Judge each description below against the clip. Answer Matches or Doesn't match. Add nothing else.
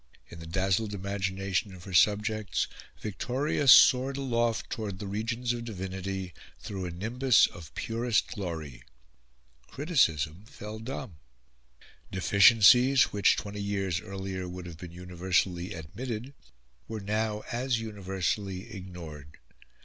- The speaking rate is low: Matches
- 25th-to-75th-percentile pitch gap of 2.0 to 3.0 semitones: Doesn't match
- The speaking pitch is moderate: Doesn't match